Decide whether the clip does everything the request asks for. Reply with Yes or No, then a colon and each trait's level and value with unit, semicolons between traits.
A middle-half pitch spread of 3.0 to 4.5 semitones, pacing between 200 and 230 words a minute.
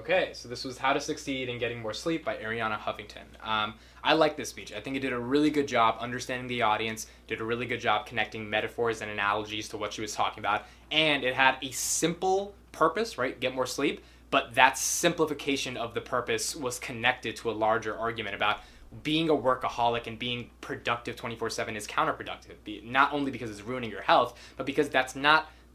Yes: average, 3.6 semitones; fast, 205 wpm